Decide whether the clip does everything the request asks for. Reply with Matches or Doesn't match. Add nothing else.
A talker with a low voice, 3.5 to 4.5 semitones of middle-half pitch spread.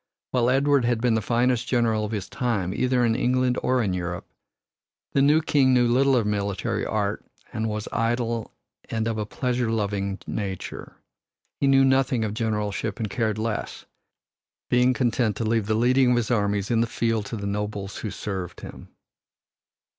Doesn't match